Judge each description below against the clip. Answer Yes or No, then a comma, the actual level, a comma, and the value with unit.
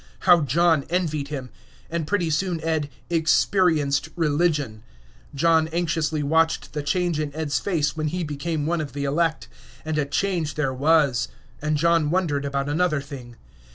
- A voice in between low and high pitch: Yes, medium, 155 Hz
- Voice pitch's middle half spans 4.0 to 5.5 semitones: No, average, 2.7 semitones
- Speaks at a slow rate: No, average, 155 wpm